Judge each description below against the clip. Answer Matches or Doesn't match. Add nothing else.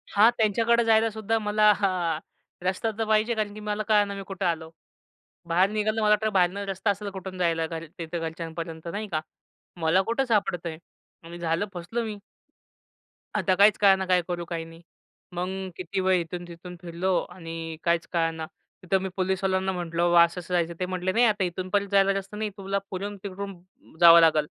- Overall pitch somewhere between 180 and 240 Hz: Matches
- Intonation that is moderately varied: Matches